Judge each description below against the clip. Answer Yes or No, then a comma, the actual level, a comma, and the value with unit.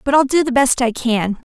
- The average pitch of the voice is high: Yes, very high, 255 Hz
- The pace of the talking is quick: Yes, fast, 275 wpm